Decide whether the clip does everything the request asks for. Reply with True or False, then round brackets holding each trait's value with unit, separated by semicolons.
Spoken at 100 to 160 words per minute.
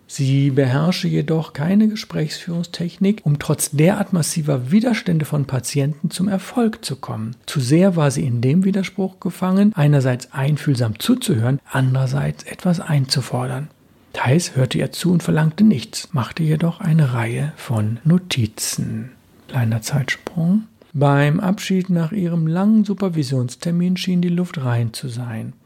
True (135 wpm)